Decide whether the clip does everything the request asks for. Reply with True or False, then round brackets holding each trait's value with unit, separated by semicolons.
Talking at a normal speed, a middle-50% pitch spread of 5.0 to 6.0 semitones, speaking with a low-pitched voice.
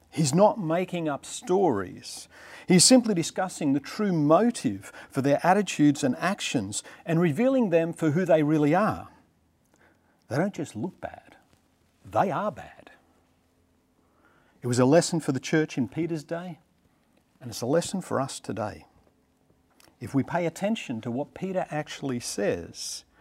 False (150 wpm; 5.3 semitones; 160 Hz)